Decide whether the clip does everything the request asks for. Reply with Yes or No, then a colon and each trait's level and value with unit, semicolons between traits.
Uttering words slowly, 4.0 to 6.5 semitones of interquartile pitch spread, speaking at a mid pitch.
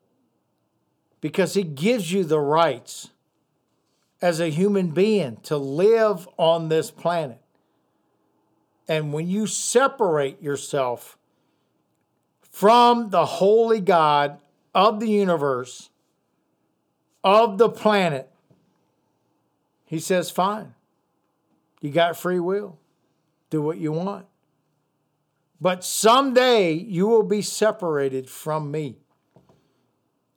Yes: slow, 95 wpm; average, 4.7 semitones; medium, 170 Hz